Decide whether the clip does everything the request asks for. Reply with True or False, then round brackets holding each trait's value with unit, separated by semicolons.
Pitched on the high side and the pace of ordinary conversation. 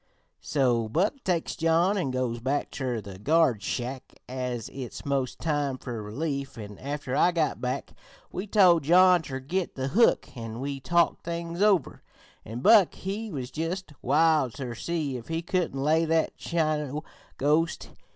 False (145 Hz; 160 wpm)